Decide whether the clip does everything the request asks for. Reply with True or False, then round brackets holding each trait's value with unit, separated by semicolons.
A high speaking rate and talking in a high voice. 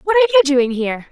True (270 wpm; 315 Hz)